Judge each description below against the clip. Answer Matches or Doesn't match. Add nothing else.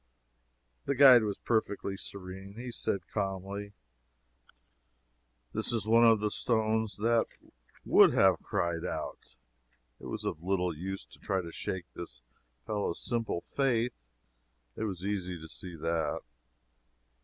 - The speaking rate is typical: Doesn't match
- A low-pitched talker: Matches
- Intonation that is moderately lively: Matches